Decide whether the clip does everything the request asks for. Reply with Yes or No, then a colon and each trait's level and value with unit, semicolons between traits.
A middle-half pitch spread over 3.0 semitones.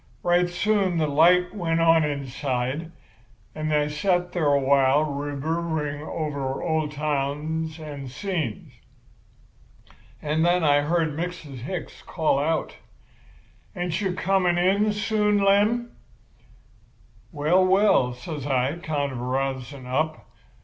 Yes: average, 3.9 semitones